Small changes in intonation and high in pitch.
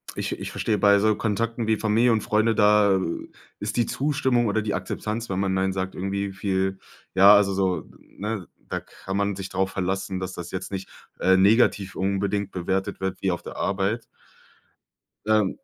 No: narrow, 2.1 semitones; low, 100 Hz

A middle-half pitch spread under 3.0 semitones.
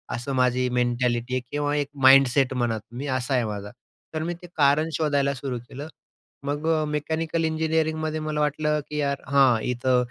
No: average, 3.5 semitones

